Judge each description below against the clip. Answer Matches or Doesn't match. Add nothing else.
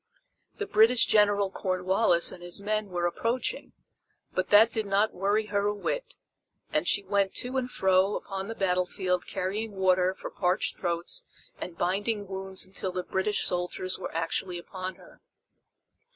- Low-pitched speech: Doesn't match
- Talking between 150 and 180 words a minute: Matches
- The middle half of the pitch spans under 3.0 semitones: Matches